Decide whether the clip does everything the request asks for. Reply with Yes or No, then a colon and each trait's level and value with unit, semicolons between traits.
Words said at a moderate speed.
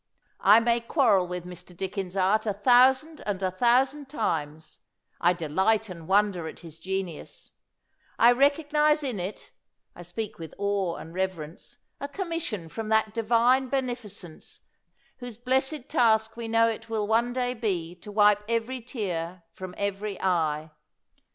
Yes: average, 155 wpm